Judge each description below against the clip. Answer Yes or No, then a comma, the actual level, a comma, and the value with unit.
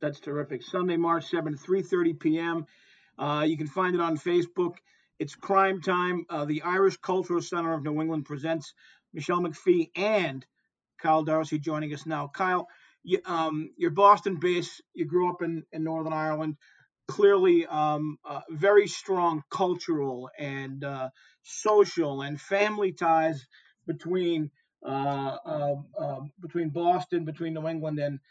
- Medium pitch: Yes, medium, 165 Hz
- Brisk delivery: No, average, 150 wpm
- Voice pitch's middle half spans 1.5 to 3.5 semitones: Yes, average, 2.8 semitones